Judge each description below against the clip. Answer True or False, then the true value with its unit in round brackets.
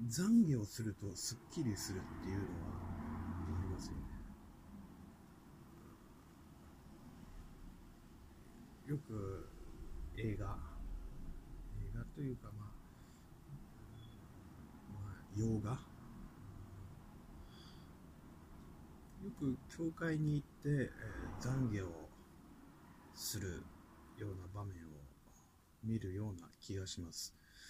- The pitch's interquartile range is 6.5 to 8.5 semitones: False (5.4 semitones)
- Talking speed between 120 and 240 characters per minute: True (145 characters per minute)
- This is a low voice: True (95 Hz)